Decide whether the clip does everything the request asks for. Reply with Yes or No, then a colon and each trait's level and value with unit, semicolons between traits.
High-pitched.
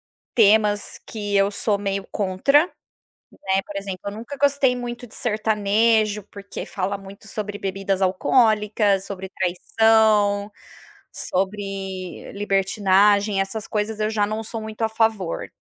Yes: high, 205 Hz